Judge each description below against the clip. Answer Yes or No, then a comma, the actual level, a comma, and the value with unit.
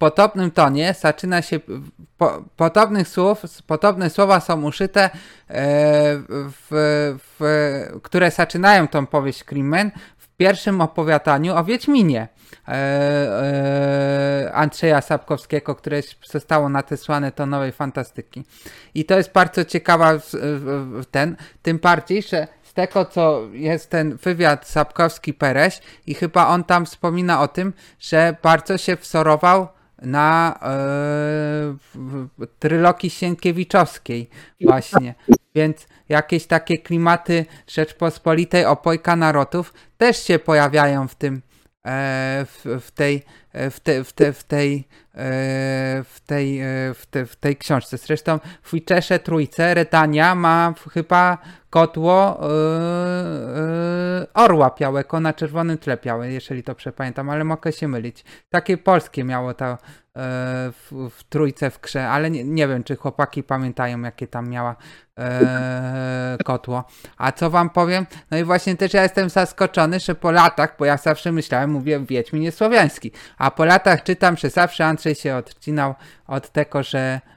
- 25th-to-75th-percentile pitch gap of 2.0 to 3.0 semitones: No, average, 3.8 semitones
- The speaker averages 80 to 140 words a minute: Yes, average, 125 wpm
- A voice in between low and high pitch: Yes, medium, 155 Hz